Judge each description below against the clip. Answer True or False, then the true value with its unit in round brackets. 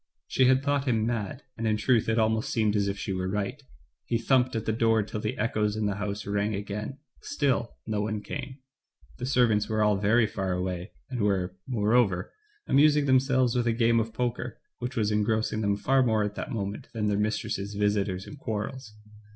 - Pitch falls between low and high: False (110 Hz)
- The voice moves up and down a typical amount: True (3.0 semitones)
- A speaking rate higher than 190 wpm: True (200 wpm)